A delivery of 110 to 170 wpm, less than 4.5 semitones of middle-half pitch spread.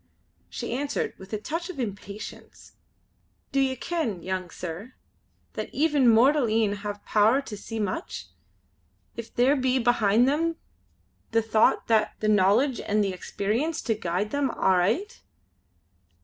No: average, 140 wpm; average, 4.8 semitones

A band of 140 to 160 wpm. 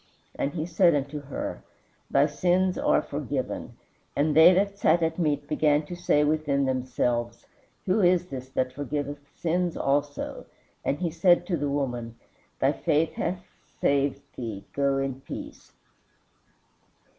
Yes: average, 145 wpm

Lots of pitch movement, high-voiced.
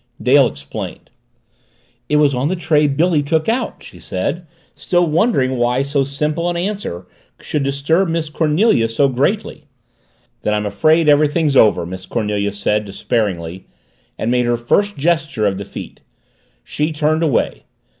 No: wide, 6.1 semitones; medium, 145 Hz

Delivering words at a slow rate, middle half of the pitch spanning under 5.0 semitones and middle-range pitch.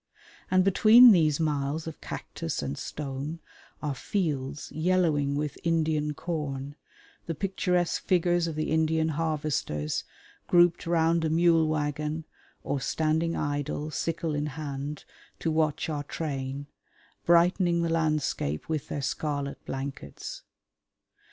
Yes: slow, 120 wpm; narrow, 2.5 semitones; medium, 155 Hz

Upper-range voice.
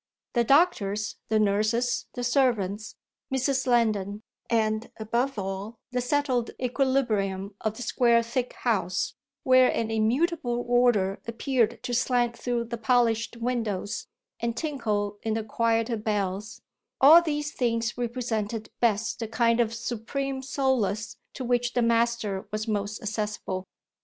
Yes: high, 230 Hz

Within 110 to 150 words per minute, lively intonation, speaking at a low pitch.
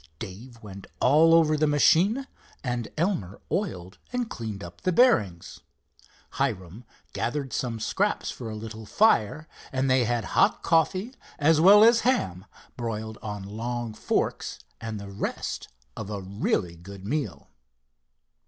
Yes: average, 140 wpm; wide, 7.4 semitones; low, 120 Hz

